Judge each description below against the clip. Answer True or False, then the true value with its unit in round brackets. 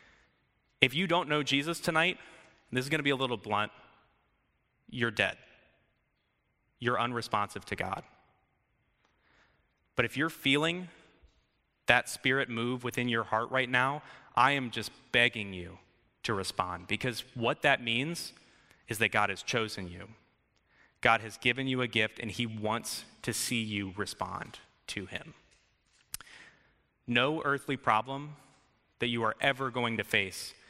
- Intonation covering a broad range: False (4.0 semitones)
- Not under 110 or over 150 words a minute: True (145 wpm)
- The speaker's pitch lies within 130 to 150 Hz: False (120 Hz)